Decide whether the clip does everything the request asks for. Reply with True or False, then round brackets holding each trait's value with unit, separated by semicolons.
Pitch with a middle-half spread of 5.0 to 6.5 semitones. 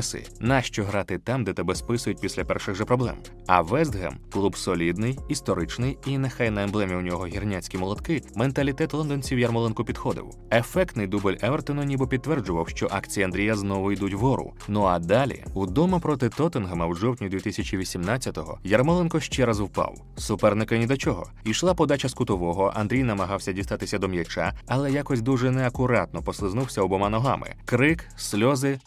True (5.3 semitones)